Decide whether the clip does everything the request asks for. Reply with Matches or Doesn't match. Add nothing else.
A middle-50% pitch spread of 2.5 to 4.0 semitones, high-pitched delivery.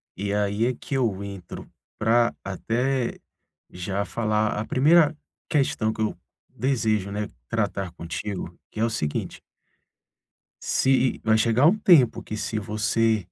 Doesn't match